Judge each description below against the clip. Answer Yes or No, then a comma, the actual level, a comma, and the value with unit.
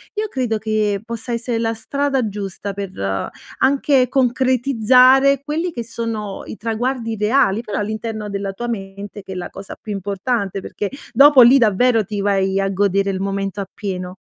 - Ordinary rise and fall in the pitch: Yes, average, 4.0 semitones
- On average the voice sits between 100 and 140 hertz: No, high, 220 Hz